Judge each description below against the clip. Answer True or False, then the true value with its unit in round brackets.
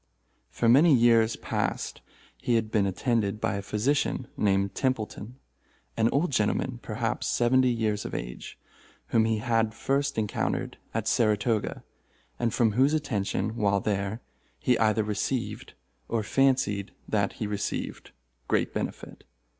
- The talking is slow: True (130 wpm)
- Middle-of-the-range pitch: False (110 Hz)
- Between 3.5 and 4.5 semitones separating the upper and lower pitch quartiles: False (3.0 semitones)